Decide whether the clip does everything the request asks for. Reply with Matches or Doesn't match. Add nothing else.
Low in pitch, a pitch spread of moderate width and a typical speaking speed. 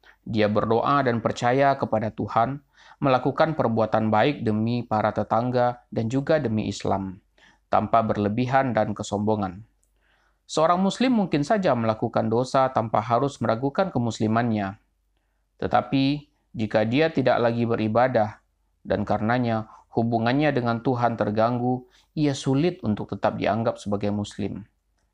Matches